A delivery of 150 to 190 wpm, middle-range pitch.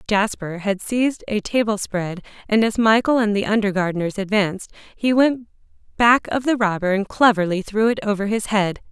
No: average, 175 wpm; high, 210 Hz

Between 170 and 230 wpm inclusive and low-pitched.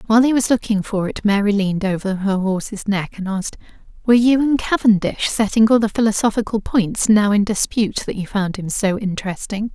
No: average, 195 wpm; high, 210 Hz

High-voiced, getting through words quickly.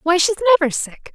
Yes: very high, 355 Hz; fast, 210 wpm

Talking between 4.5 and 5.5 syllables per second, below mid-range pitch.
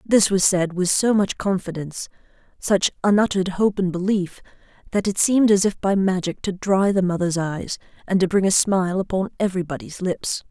No: 5.4 syllables/s; high, 190 Hz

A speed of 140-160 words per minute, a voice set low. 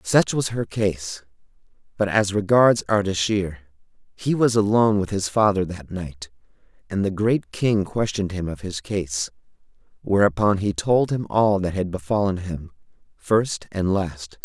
Yes: average, 155 wpm; low, 100 Hz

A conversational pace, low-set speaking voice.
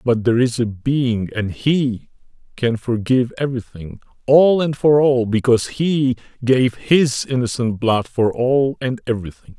Yes: average, 150 wpm; low, 125 Hz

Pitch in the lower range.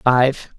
Yes: low, 130 Hz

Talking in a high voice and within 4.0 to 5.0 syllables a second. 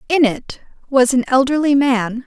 Yes: very high, 260 Hz; 4.5 syllables/s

